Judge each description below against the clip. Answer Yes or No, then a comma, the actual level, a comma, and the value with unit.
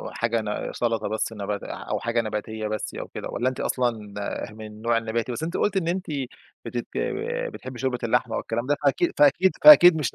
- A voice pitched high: No, low, 120 Hz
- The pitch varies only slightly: No, average, 4.2 semitones